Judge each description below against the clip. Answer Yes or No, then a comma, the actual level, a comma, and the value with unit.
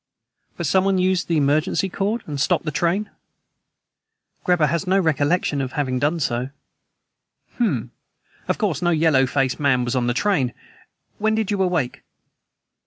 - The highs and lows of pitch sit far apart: Yes, wide, 5.7 semitones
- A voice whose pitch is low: No, medium, 160 Hz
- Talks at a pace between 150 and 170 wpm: Yes, average, 155 wpm